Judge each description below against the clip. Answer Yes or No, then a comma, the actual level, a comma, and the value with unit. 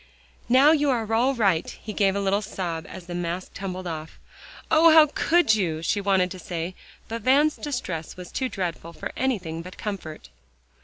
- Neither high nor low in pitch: No, high, 195 Hz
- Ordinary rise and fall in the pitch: No, wide, 6.3 semitones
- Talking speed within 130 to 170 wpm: No, average, 185 wpm